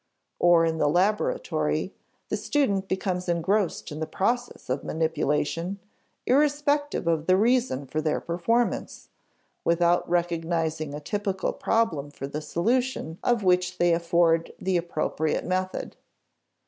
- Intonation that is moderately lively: Yes, average, 4.2 semitones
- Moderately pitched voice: Yes, medium, 175 Hz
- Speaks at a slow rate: Yes, slow, 125 wpm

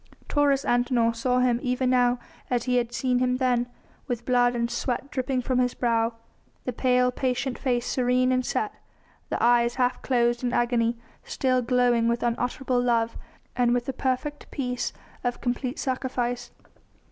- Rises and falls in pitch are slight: Yes, narrow, 1.0 semitones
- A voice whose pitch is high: Yes, high, 245 Hz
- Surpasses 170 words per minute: No, average, 160 wpm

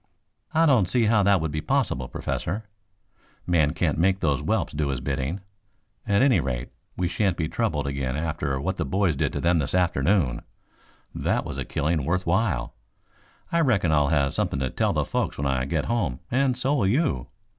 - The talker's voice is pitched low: Yes, very low, 80 Hz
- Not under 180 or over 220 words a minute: Yes, average, 195 wpm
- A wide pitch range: Yes, wide, 6.4 semitones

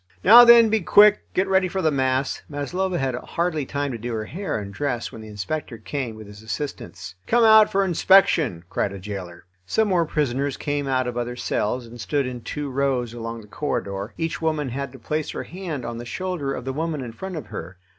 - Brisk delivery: Yes, fast, 220 wpm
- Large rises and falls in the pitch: Yes, wide, 6.3 semitones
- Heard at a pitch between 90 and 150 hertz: Yes, medium, 140 Hz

